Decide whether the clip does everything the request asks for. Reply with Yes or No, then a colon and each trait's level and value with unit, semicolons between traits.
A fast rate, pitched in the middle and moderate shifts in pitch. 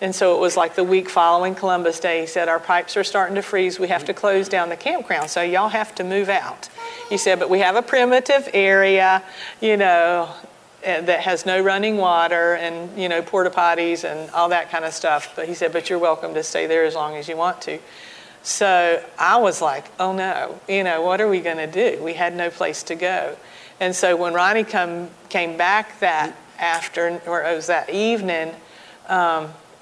No: fast, 215 wpm; medium, 180 Hz; narrow, 2.2 semitones